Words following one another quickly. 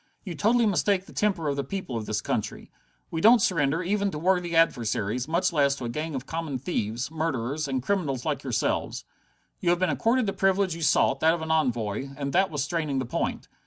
Yes: fast, 215 wpm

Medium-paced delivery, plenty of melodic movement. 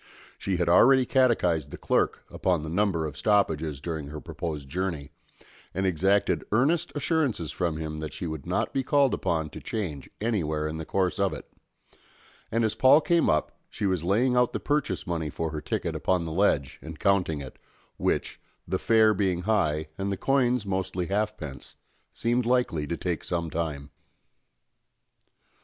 Yes: average, 170 wpm; wide, 5.8 semitones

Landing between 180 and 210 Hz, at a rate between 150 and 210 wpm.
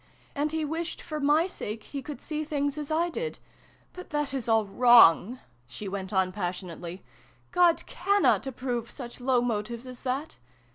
No: very high, 255 Hz; average, 180 wpm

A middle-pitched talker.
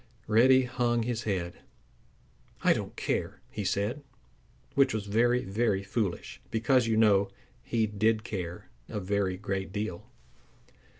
No: low, 110 Hz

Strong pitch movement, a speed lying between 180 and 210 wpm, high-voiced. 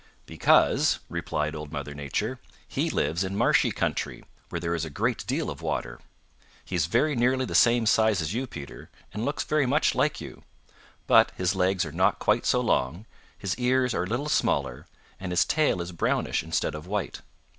No: wide, 7.4 semitones; average, 190 wpm; very low, 95 Hz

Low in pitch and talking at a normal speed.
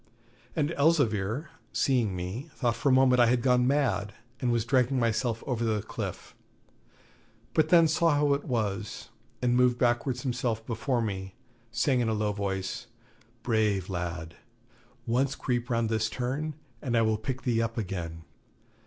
Yes: low, 120 Hz; average, 160 wpm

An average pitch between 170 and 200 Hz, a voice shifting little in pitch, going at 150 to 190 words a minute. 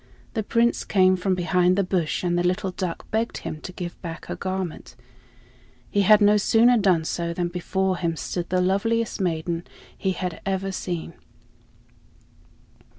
Yes: medium, 185 Hz; narrow, 2.2 semitones; average, 160 wpm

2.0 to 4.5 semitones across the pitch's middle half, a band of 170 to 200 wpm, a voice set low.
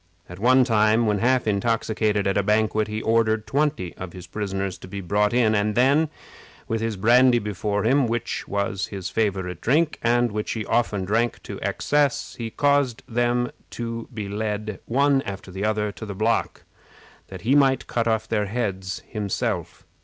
Yes: average, 2.9 semitones; average, 175 wpm; low, 110 Hz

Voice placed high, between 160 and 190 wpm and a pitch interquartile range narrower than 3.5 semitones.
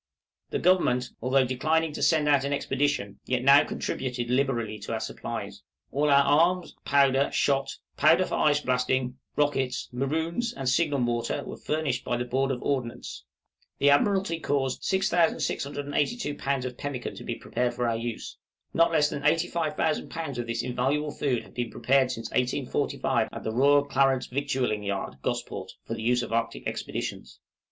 No: low, 135 Hz; average, 170 wpm; average, 3.0 semitones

